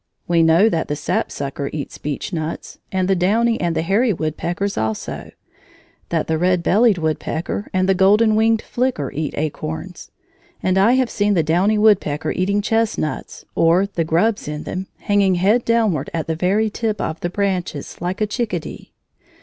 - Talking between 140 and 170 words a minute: Yes, average, 165 wpm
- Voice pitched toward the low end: No, medium, 185 Hz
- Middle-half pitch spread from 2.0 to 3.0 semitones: No, average, 4.6 semitones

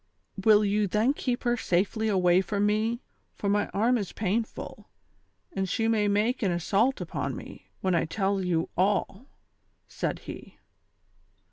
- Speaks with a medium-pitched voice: No, high, 205 Hz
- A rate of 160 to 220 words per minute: Yes, average, 165 wpm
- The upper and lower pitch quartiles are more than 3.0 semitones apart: No, average, 2.7 semitones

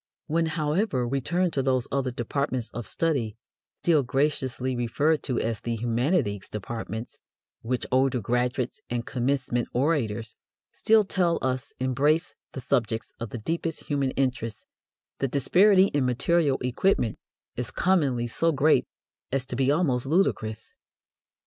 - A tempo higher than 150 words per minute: No, slow, 135 wpm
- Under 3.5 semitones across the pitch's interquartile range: No, average, 4.2 semitones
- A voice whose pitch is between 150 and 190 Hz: No, low, 130 Hz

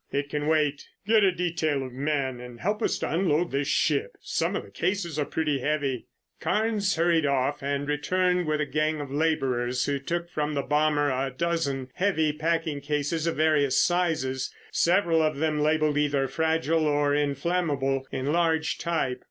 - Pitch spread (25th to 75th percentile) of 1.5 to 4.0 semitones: Yes, average, 2.8 semitones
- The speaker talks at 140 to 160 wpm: No, average, 175 wpm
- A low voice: No, medium, 150 Hz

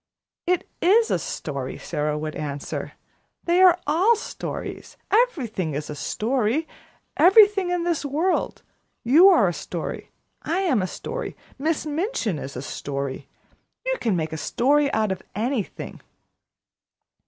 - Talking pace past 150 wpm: No, average, 140 wpm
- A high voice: Yes, very high, 280 Hz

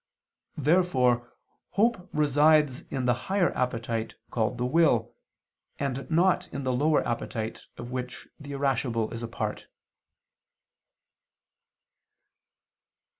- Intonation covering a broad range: No, average, 4.3 semitones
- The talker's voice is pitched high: No, low, 130 Hz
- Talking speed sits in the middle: No, slow, 105 wpm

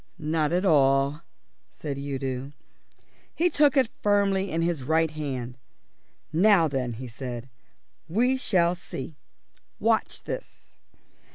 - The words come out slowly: Yes, slow, 115 wpm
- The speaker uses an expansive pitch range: Yes, wide, 5.8 semitones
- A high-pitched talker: No, medium, 155 Hz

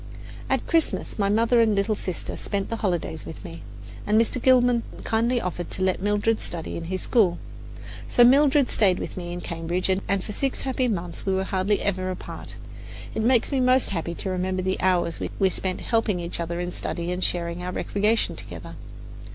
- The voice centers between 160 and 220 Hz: Yes, high, 190 Hz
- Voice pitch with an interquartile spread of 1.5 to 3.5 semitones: No, average, 4.2 semitones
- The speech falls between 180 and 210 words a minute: Yes, average, 190 wpm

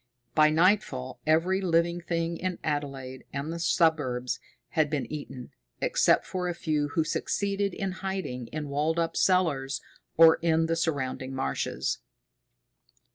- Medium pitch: Yes, medium, 160 Hz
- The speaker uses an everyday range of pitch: Yes, average, 3.6 semitones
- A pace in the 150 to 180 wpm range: No, slow, 135 wpm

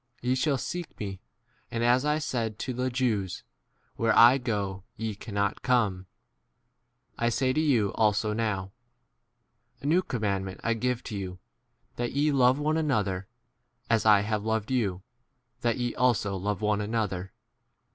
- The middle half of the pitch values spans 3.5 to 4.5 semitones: Yes, average, 3.9 semitones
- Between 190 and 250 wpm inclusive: No, average, 160 wpm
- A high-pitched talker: No, low, 115 Hz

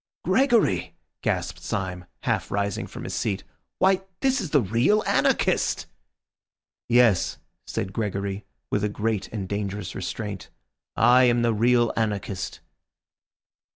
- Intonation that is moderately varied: Yes, average, 3.8 semitones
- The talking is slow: Yes, slow, 120 wpm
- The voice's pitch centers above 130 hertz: No, low, 105 Hz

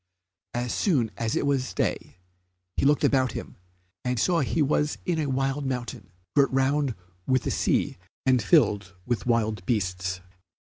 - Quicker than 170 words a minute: No, average, 155 wpm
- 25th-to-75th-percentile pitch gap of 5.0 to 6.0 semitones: No, average, 4.1 semitones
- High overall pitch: No, low, 130 Hz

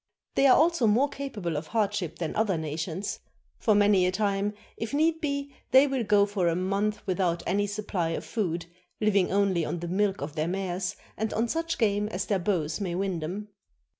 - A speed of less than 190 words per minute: No, average, 195 wpm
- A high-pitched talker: Yes, high, 200 Hz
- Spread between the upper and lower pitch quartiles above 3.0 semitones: Yes, average, 3.7 semitones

